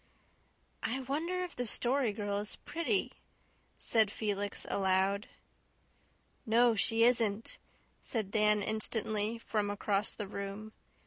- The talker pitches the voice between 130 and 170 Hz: No, high, 215 Hz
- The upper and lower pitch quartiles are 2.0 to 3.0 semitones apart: Yes, narrow, 2.5 semitones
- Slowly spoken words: Yes, slow, 115 wpm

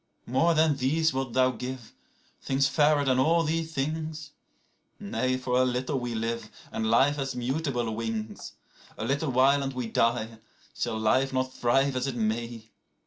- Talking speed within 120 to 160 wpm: Yes, average, 155 wpm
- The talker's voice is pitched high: No, low, 130 Hz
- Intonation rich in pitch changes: No, average, 3.3 semitones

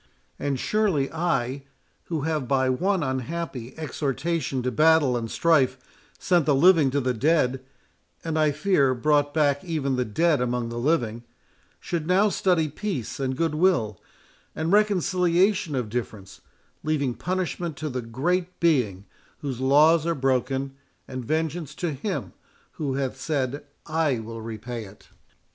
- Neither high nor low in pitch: Yes, medium, 145 Hz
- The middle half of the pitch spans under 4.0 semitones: No, average, 4.5 semitones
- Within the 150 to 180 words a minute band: No, average, 140 wpm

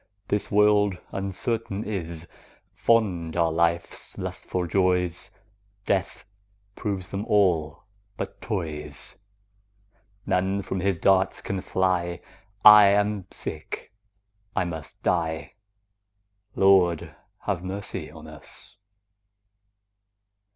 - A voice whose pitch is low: Yes, very low, 95 Hz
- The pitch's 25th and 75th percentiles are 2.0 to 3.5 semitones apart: Yes, average, 2.9 semitones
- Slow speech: Yes, slow, 95 wpm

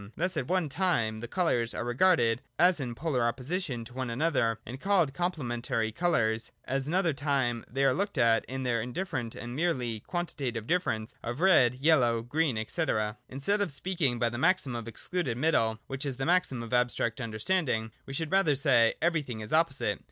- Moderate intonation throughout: No, wide, 5.9 semitones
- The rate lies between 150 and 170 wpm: No, average, 190 wpm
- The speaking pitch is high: No, low, 130 Hz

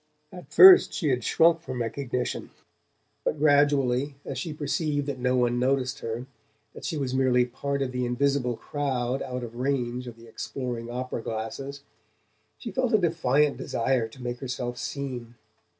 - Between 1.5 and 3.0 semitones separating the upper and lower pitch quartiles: Yes, narrow, 2.5 semitones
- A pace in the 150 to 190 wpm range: Yes, average, 165 wpm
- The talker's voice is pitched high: No, low, 130 Hz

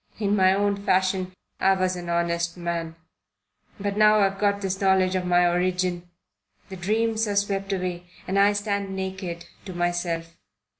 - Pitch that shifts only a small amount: Yes, narrow, 2.3 semitones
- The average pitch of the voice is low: No, high, 190 Hz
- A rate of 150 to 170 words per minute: Yes, average, 160 wpm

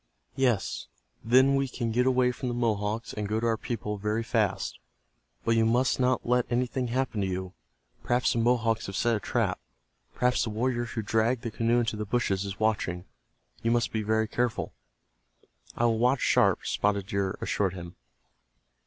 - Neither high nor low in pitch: No, low, 115 Hz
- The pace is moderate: Yes, average, 180 wpm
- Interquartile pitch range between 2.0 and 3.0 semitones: Yes, average, 2.7 semitones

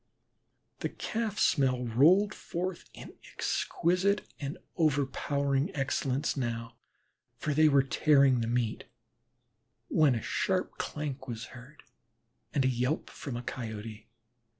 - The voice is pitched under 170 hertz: Yes, medium, 140 Hz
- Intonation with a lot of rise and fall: No, average, 4.1 semitones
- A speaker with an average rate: No, slow, 120 wpm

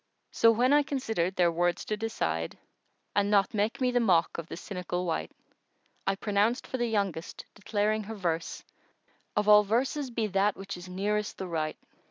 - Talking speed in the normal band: Yes, average, 190 wpm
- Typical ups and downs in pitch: Yes, average, 4.0 semitones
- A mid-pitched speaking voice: No, high, 205 Hz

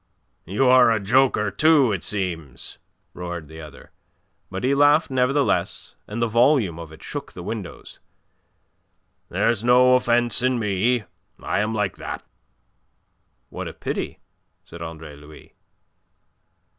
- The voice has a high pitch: No, low, 110 Hz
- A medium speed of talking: No, slow, 130 wpm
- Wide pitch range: Yes, wide, 6.4 semitones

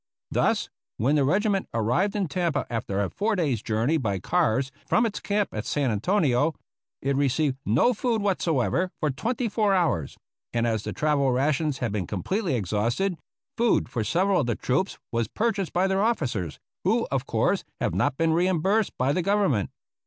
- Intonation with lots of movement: Yes, wide, 8.3 semitones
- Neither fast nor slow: Yes, average, 175 wpm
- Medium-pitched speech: Yes, medium, 150 Hz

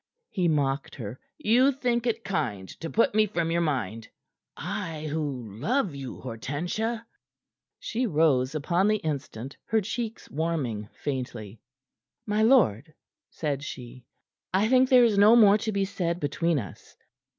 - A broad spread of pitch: Yes, wide, 8.1 semitones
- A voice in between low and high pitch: Yes, medium, 165 Hz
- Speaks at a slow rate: No, average, 145 wpm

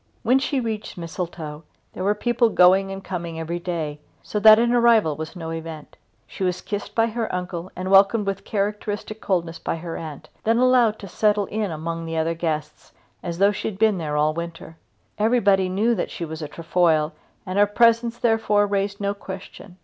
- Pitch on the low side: No, high, 190 Hz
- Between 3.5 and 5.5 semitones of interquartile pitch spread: Yes, average, 4.4 semitones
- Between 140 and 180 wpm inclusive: No, average, 195 wpm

